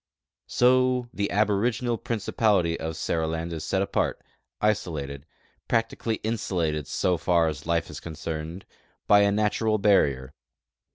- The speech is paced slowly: Yes, slow, 125 wpm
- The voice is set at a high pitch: No, very low, 95 Hz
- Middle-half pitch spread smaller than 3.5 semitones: No, average, 5.0 semitones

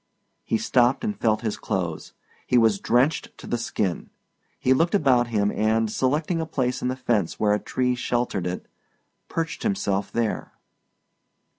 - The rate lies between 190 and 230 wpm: No, average, 160 wpm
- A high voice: No, low, 120 Hz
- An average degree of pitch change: Yes, average, 3.9 semitones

